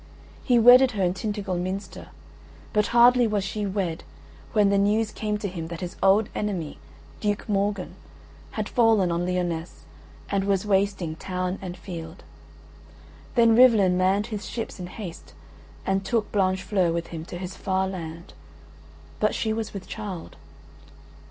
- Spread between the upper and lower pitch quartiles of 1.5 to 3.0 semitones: Yes, average, 2.7 semitones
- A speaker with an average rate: Yes, average, 150 wpm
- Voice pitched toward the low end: No, high, 195 Hz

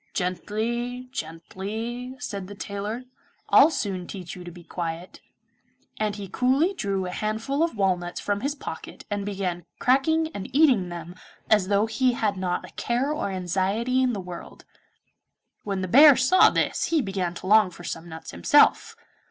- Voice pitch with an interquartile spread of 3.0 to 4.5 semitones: No, wide, 5.4 semitones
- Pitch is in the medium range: No, high, 205 Hz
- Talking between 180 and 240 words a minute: No, average, 170 wpm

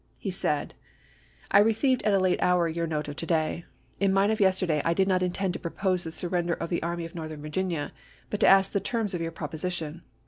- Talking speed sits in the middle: No, fast, 235 wpm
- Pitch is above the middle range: No, medium, 175 Hz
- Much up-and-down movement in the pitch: No, average, 2.8 semitones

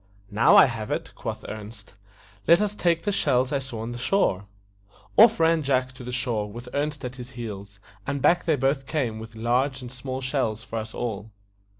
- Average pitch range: Yes, average, 3.9 semitones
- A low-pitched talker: Yes, low, 125 Hz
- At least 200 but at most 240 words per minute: Yes, fast, 205 wpm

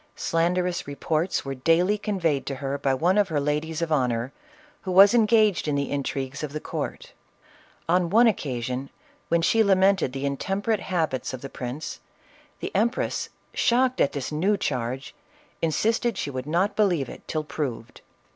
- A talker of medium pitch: Yes, medium, 160 Hz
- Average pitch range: No, wide, 5.9 semitones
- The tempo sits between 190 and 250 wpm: No, average, 165 wpm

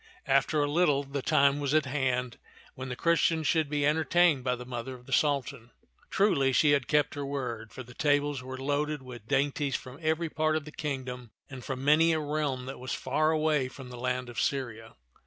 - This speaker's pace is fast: Yes, fast, 210 wpm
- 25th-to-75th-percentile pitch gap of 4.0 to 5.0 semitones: No, average, 2.9 semitones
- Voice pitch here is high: No, medium, 140 Hz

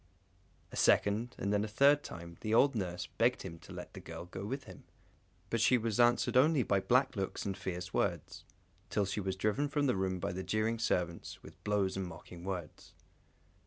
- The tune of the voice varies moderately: Yes, average, 4.4 semitones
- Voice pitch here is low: Yes, low, 100 Hz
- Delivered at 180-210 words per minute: Yes, average, 200 wpm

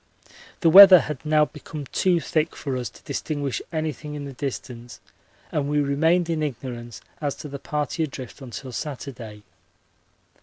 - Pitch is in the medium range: Yes, medium, 145 Hz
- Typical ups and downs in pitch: Yes, average, 3.0 semitones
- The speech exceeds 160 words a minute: No, average, 155 wpm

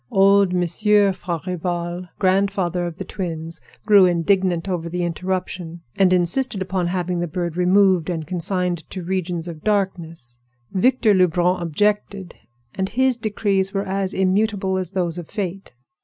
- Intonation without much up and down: Yes, narrow, 2.2 semitones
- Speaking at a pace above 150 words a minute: No, average, 140 wpm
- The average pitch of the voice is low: No, medium, 185 Hz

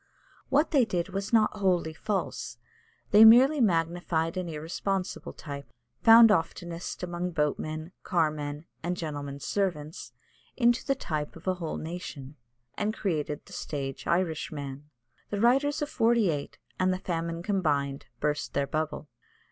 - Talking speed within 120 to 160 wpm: Yes, average, 140 wpm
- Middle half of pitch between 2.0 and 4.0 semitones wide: No, average, 5.1 semitones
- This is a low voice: No, medium, 170 Hz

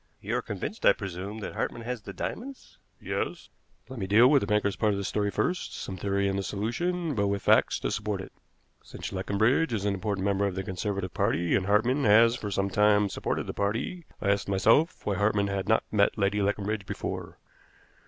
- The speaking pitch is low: Yes, low, 100 Hz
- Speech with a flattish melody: Yes, narrow, 2.2 semitones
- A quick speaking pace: Yes, fast, 210 wpm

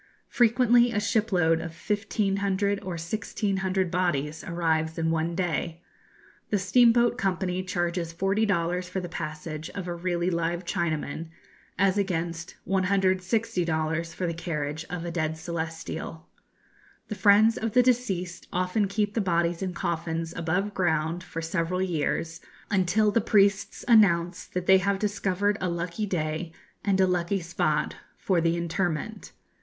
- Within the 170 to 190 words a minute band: No, average, 145 wpm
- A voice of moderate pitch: Yes, medium, 180 Hz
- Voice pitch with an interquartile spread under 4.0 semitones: Yes, average, 3.2 semitones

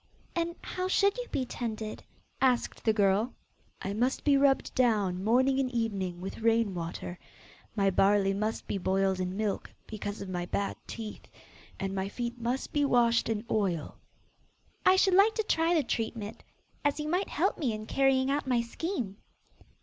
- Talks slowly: No, average, 175 wpm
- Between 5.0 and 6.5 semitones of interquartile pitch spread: Yes, wide, 5.4 semitones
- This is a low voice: No, high, 230 Hz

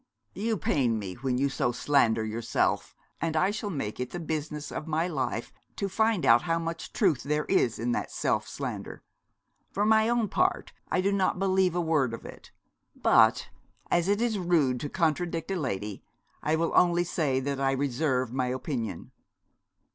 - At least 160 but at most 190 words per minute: Yes, average, 180 wpm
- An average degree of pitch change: No, wide, 6.1 semitones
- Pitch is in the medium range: Yes, medium, 155 Hz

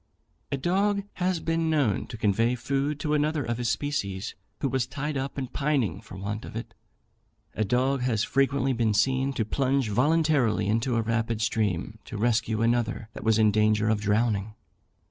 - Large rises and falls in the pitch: No, average, 4.3 semitones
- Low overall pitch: Yes, low, 120 Hz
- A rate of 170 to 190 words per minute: Yes, average, 180 wpm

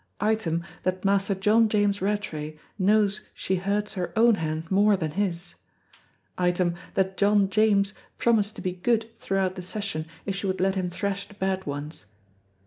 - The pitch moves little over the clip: Yes, narrow, 2.3 semitones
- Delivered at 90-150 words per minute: No, average, 165 wpm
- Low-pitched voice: No, high, 195 Hz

